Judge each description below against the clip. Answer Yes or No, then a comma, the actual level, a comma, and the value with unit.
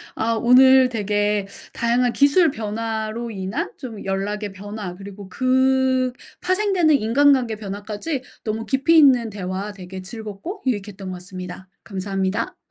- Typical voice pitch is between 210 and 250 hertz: Yes, high, 220 Hz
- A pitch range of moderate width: Yes, average, 4.7 semitones